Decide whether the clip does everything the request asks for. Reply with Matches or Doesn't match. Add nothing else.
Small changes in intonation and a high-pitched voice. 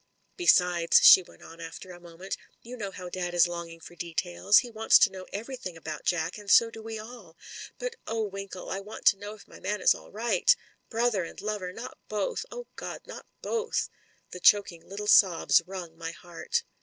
Doesn't match